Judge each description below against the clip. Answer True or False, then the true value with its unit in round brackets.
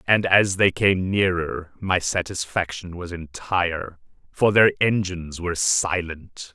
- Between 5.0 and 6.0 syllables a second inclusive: False (4.0 syllables/s)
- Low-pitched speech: True (90 Hz)